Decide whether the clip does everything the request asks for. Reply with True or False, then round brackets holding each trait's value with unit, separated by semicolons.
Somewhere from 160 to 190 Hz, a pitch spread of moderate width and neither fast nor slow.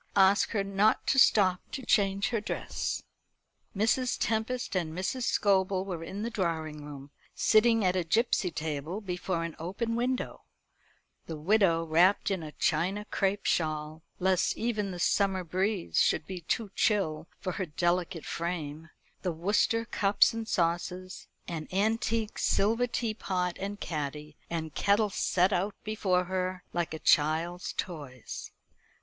True (185 Hz; 3.9 semitones; 145 wpm)